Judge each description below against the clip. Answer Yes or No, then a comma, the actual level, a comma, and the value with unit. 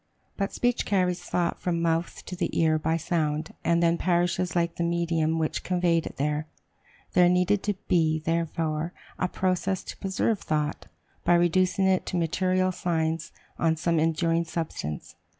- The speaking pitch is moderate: Yes, medium, 170 Hz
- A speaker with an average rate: Yes, average, 165 wpm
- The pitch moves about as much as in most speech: No, narrow, 1.9 semitones